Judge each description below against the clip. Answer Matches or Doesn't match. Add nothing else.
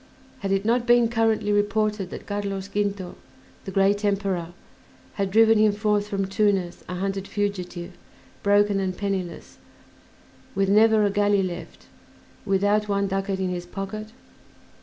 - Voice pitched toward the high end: Matches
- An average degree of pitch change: Doesn't match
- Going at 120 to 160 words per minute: Matches